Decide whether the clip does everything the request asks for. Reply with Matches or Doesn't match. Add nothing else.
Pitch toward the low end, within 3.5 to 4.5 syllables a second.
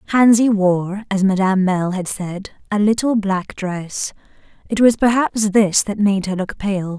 Doesn't match